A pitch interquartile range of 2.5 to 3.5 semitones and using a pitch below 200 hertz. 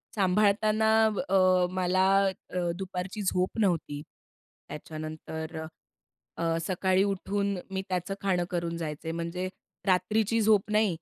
Yes: average, 3.0 semitones; medium, 185 Hz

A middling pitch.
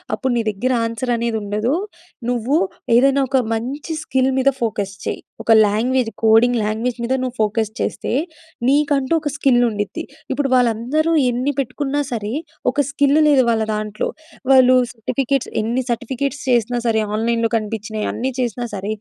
No: high, 245 Hz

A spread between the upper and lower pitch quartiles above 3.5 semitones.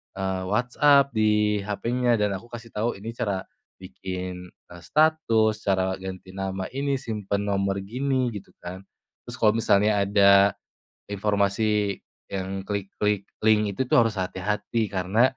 No: average, 2.9 semitones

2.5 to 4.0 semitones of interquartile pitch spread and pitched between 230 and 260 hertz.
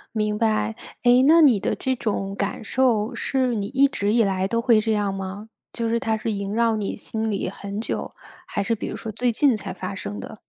No: average, 2.8 semitones; high, 220 Hz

